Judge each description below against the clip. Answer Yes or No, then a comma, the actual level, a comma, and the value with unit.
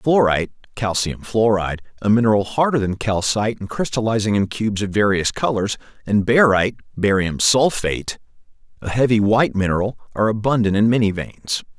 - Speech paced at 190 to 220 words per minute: No, average, 145 wpm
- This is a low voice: Yes, low, 110 Hz